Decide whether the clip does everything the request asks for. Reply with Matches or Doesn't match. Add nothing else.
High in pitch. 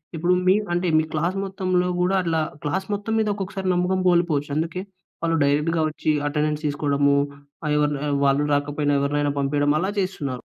Doesn't match